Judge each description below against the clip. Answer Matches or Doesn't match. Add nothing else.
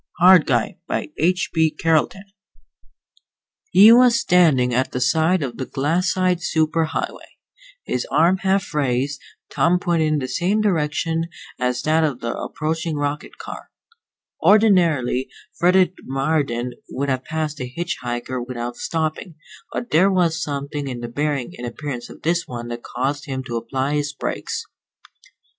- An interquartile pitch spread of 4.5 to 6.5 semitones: Matches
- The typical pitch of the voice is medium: Matches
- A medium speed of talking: Matches